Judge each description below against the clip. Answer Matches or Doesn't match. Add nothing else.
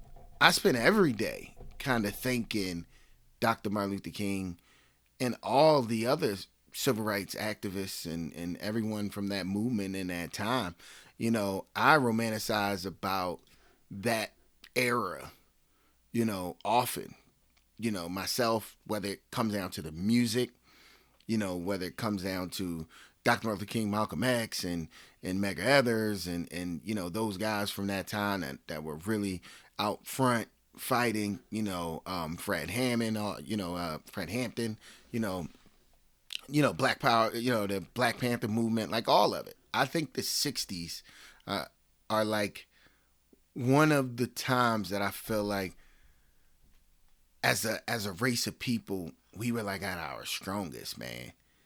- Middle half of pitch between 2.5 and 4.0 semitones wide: Doesn't match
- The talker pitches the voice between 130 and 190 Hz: Doesn't match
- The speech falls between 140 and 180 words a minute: Matches